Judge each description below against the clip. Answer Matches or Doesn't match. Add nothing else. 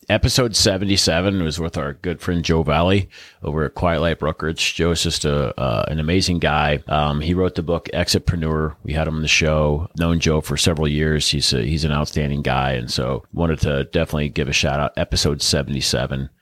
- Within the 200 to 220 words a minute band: Matches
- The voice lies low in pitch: Matches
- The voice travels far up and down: Doesn't match